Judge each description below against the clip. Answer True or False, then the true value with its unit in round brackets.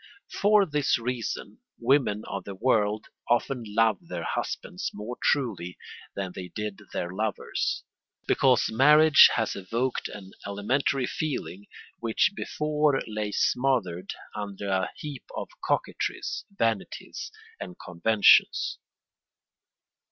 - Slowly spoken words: True (110 wpm)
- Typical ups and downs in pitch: True (5.0 semitones)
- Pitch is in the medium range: False (110 Hz)